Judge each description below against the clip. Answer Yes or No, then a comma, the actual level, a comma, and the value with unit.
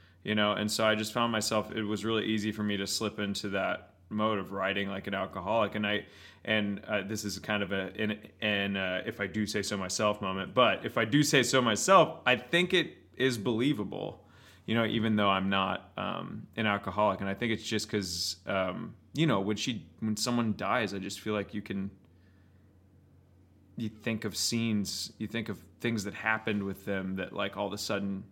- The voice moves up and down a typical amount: No, narrow, 2.0 semitones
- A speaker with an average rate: No, fast, 210 wpm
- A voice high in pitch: No, low, 105 Hz